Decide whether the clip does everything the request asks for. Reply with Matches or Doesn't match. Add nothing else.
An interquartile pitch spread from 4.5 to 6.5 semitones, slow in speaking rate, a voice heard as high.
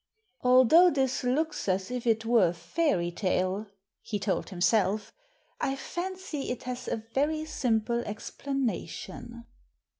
Matches